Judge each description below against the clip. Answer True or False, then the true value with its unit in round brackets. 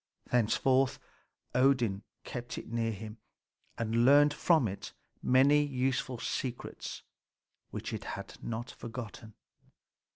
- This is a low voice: True (120 Hz)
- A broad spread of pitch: False (2.9 semitones)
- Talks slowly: True (105 wpm)